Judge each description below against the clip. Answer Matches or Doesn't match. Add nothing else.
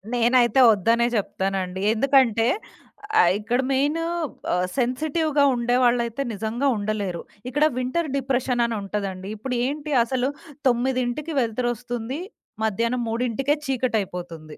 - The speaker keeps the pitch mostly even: Doesn't match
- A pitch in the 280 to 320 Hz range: Doesn't match